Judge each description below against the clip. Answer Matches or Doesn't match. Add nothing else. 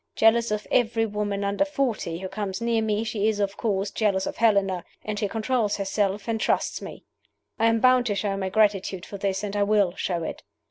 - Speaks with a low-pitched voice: Doesn't match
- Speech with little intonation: Matches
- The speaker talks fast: Matches